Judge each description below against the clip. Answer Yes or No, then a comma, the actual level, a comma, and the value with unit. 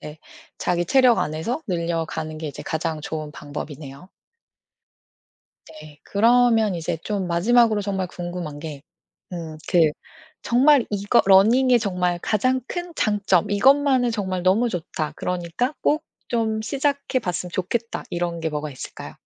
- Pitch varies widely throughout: Yes, wide, 6.4 semitones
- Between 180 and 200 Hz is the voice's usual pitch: Yes, medium, 185 Hz